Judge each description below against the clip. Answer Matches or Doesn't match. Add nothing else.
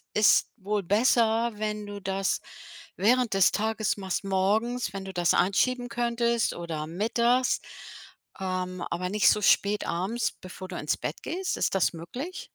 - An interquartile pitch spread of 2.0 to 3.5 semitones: Doesn't match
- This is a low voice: Doesn't match